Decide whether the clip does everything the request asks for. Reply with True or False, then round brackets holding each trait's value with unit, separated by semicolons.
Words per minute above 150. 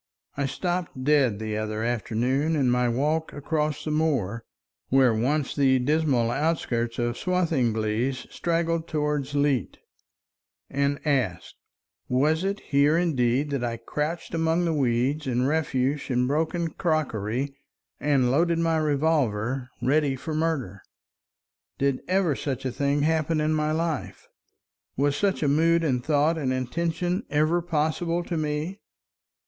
False (135 wpm)